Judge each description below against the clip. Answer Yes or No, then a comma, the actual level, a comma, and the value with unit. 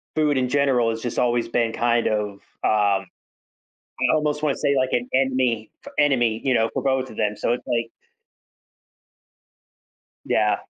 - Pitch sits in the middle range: No, low, 120 Hz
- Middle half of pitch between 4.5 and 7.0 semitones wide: No, average, 2.9 semitones